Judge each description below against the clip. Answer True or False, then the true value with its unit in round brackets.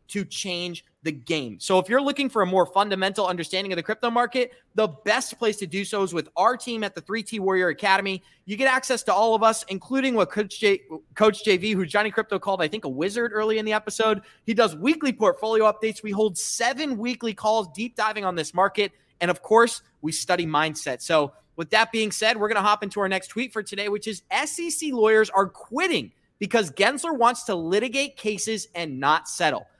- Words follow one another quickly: True (220 wpm)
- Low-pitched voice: False (210 Hz)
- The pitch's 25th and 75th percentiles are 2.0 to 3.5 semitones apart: True (3.2 semitones)